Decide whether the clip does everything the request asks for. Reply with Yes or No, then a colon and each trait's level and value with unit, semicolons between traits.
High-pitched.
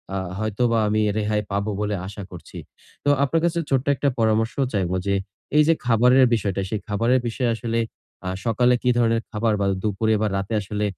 No: low, 110 Hz